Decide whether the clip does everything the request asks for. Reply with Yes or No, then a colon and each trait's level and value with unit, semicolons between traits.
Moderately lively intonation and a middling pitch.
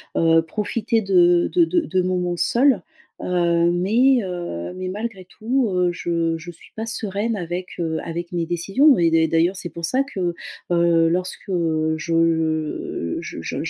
Yes: average, 4.1 semitones; medium, 175 Hz